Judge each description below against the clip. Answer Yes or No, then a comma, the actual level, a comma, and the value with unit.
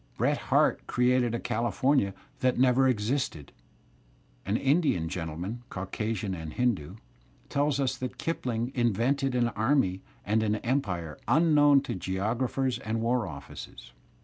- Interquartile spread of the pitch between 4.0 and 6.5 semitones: Yes, average, 5.1 semitones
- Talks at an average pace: No, slow, 125 wpm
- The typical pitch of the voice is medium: No, low, 120 Hz